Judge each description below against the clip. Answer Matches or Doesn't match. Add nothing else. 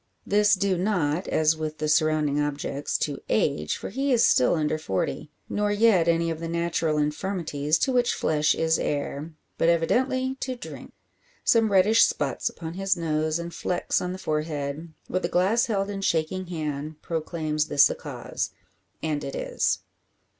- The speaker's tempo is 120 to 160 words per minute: Doesn't match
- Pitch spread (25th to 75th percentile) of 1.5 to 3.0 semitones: Doesn't match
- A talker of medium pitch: Matches